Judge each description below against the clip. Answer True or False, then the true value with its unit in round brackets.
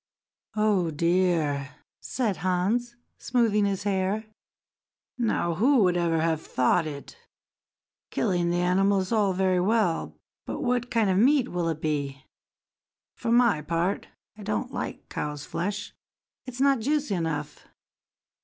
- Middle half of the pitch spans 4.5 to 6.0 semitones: True (5.0 semitones)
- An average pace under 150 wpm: True (135 wpm)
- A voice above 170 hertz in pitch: True (190 Hz)